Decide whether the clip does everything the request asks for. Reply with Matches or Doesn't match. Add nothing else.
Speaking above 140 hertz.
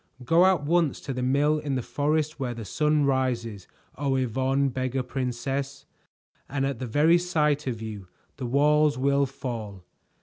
Doesn't match